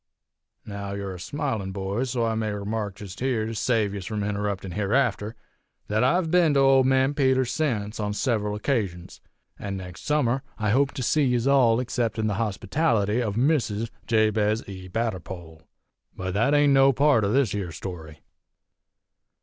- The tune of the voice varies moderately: Yes, average, 4.7 semitones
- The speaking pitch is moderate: No, low, 110 Hz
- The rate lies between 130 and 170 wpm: Yes, average, 165 wpm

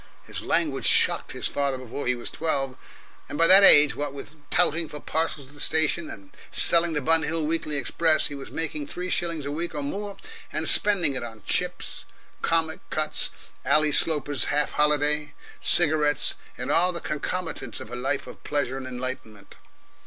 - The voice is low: No, medium, 150 Hz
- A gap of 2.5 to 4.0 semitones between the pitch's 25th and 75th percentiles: Yes, average, 2.8 semitones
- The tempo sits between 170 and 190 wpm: Yes, average, 180 wpm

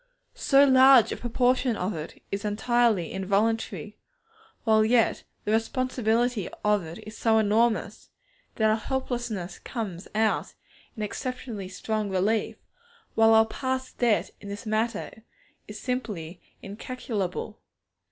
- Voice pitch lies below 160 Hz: No, high, 220 Hz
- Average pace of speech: No, slow, 125 wpm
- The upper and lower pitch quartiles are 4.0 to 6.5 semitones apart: No, average, 2.9 semitones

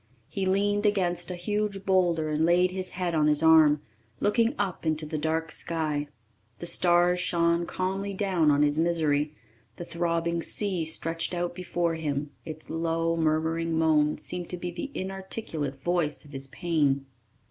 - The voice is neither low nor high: Yes, medium, 170 Hz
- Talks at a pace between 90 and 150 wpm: No, average, 160 wpm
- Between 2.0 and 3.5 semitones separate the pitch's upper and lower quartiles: Yes, narrow, 2.5 semitones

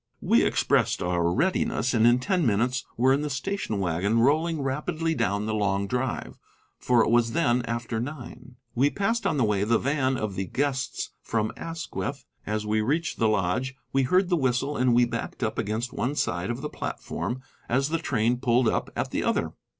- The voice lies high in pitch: No, low, 125 Hz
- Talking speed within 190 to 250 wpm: Yes, average, 195 wpm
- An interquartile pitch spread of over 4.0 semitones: Yes, average, 4.4 semitones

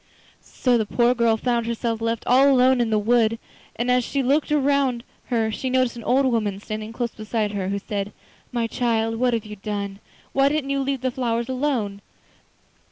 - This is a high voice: Yes, high, 235 Hz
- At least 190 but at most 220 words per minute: Yes, average, 195 wpm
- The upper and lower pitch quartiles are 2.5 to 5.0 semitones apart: Yes, average, 2.8 semitones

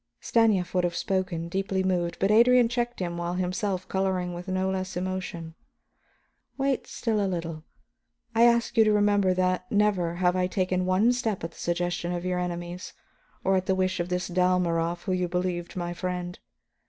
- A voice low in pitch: No, medium, 185 Hz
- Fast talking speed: No, average, 185 wpm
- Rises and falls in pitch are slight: Yes, narrow, 1.7 semitones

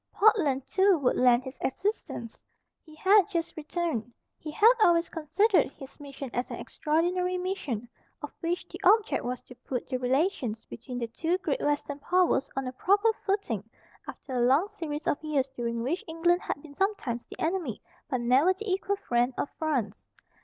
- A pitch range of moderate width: No, wide, 6.4 semitones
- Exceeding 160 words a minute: Yes, average, 175 wpm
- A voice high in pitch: Yes, very high, 305 Hz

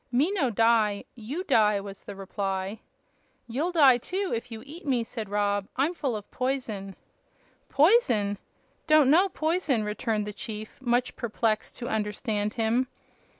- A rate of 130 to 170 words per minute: Yes, average, 150 wpm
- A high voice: Yes, high, 230 Hz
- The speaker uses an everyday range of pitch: Yes, average, 4.7 semitones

